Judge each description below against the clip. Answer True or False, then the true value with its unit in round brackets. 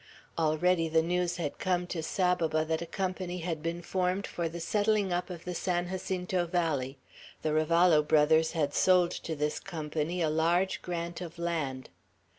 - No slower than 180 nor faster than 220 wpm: False (170 wpm)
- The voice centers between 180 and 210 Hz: False (170 Hz)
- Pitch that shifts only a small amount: True (2.2 semitones)